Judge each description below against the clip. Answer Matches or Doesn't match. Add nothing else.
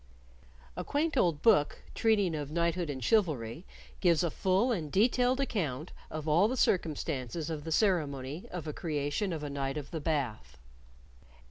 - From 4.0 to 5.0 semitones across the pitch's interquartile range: Matches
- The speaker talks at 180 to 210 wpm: Doesn't match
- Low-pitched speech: Doesn't match